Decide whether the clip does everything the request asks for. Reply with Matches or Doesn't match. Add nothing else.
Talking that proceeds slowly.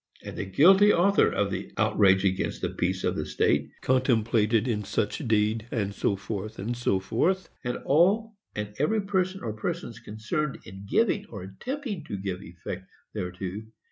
Doesn't match